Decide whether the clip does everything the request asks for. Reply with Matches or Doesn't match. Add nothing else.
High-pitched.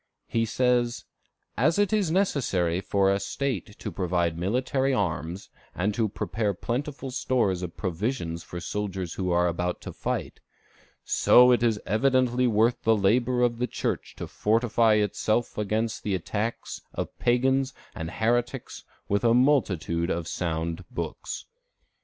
Doesn't match